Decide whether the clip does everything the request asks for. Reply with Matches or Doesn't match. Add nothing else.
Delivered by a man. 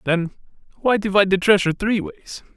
Matches